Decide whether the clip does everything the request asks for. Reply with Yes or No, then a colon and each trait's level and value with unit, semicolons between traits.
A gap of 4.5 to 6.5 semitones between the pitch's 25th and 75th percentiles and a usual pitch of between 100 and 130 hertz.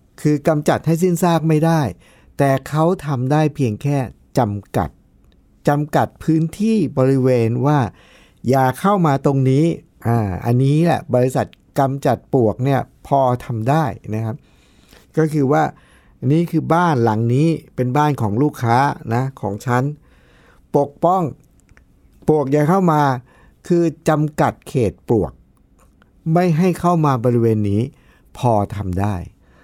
No: average, 4.9 semitones; medium, 140 Hz